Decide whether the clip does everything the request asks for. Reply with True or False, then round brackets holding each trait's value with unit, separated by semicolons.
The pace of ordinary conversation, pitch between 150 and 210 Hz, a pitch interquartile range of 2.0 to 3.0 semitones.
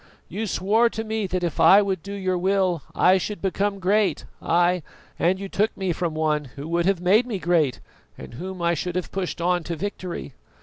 False (210 wpm; 185 Hz; 2.5 semitones)